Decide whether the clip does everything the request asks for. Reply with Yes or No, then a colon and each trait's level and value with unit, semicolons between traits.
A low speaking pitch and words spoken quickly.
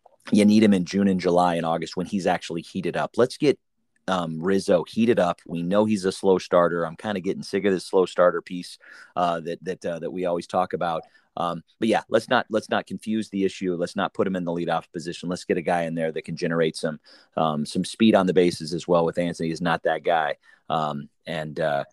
Yes: very low, 85 Hz; fast, 245 wpm